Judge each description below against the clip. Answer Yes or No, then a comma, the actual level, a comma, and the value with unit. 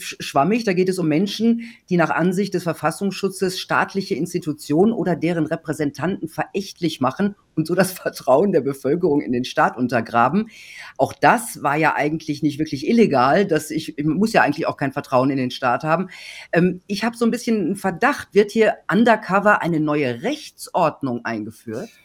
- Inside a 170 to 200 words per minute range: Yes, average, 175 wpm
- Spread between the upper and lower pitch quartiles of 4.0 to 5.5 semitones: Yes, average, 5.1 semitones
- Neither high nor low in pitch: Yes, medium, 165 Hz